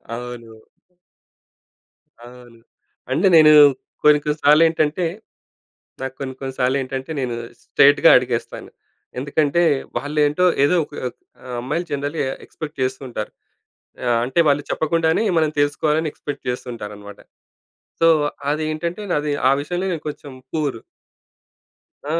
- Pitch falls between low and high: Yes, medium, 145 Hz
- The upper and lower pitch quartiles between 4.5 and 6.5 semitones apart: No, average, 3.5 semitones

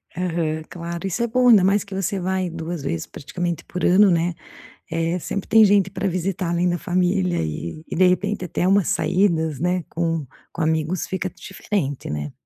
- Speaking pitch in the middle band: Yes, medium, 180 Hz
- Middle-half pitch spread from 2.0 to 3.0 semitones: Yes, average, 2.7 semitones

